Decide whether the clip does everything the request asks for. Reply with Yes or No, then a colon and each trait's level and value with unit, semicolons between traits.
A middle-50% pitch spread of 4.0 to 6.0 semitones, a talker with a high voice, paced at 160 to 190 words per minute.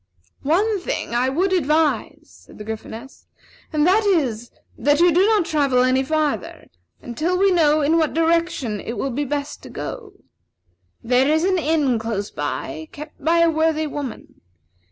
Yes: average, 4.7 semitones; very high, 300 Hz; average, 170 wpm